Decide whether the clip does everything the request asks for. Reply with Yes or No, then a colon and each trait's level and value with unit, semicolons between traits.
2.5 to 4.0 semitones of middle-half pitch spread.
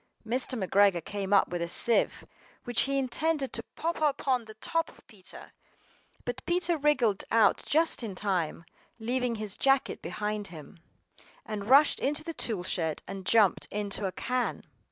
No: wide, 5.4 semitones